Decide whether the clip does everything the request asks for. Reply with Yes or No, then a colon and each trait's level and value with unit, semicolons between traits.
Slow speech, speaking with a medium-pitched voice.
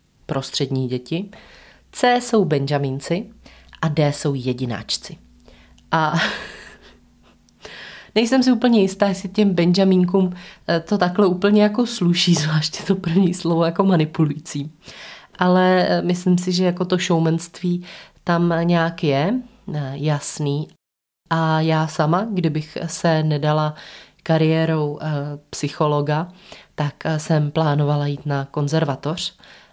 Yes: slow, 105 wpm; medium, 165 Hz